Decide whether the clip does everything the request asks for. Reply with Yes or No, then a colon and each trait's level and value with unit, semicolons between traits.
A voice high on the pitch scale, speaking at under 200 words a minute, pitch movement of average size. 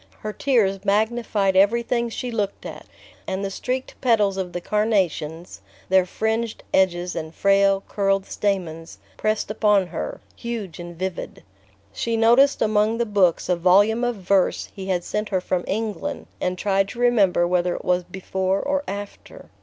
Yes: high, 195 Hz; average, 160 wpm; average, 3.3 semitones